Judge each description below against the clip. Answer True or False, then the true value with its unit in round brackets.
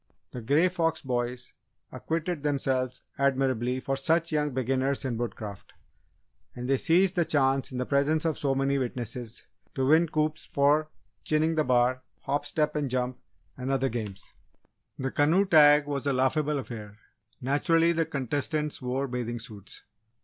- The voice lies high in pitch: False (135 Hz)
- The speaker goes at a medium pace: True (155 wpm)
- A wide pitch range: False (3.2 semitones)